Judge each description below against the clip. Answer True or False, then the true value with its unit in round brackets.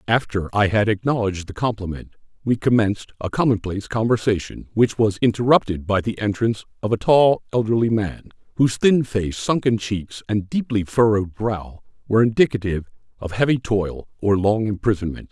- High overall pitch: False (110 Hz)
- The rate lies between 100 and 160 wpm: True (155 wpm)